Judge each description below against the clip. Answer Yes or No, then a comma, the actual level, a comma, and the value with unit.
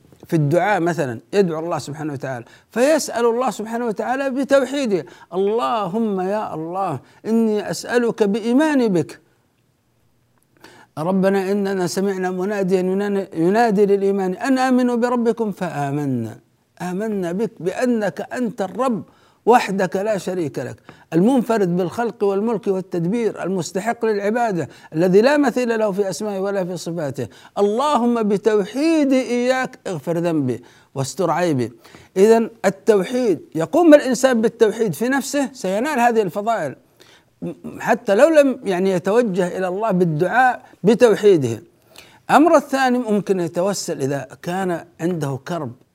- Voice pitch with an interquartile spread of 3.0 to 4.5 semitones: No, average, 5.0 semitones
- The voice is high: Yes, high, 200 Hz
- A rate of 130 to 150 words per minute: No, average, 115 wpm